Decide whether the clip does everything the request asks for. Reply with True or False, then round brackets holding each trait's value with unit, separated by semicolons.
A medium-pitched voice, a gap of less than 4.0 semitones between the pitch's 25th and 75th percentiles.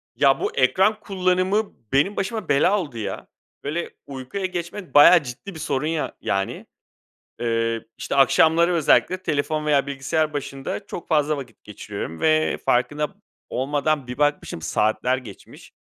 False (150 Hz; 4.8 semitones)